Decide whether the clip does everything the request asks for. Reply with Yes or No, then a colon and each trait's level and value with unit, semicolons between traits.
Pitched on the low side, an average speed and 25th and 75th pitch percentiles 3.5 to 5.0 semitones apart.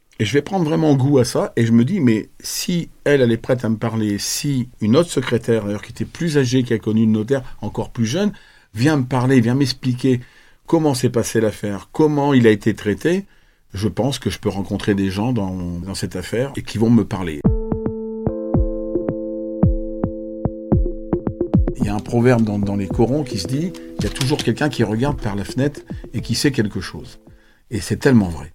Yes: low, 115 Hz; average, 210 wpm; average, 4.1 semitones